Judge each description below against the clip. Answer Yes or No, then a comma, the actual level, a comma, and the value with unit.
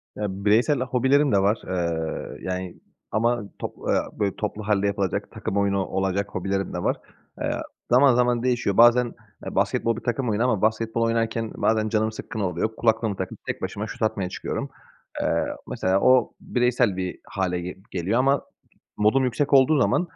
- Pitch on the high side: No, low, 110 Hz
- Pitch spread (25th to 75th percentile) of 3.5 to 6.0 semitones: Yes, average, 3.9 semitones